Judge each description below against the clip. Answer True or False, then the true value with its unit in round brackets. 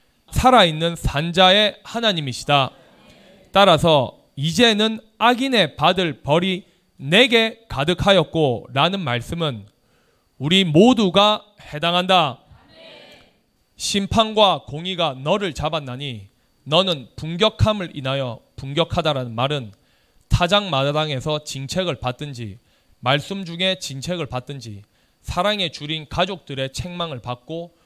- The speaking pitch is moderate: True (160 Hz)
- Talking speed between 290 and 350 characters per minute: False (240 characters per minute)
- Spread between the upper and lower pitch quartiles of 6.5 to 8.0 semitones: False (5.7 semitones)